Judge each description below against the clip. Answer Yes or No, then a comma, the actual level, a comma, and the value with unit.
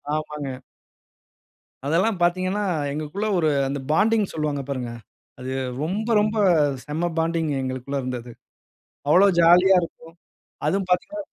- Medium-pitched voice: Yes, medium, 165 Hz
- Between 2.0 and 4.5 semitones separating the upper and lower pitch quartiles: No, average, 5.0 semitones